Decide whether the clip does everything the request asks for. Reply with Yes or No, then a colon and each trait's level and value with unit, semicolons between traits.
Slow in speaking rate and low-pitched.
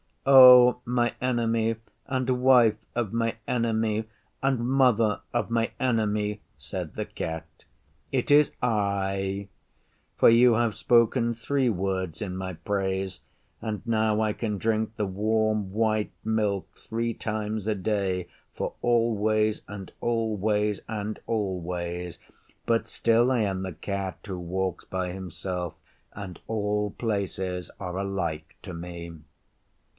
Yes: slow, 130 wpm; low, 105 Hz